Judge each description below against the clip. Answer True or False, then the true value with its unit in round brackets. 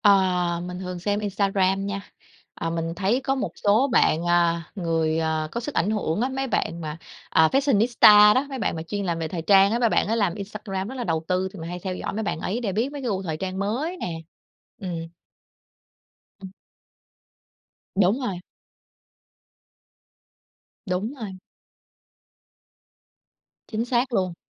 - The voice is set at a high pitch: True (195 Hz)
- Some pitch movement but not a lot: True (4.3 semitones)